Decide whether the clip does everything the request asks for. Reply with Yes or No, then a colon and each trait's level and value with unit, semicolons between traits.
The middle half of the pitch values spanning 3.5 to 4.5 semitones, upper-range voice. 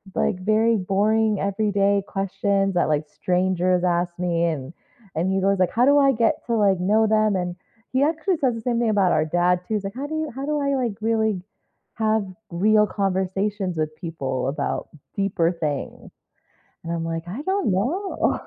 Yes: average, 3.9 semitones; high, 195 Hz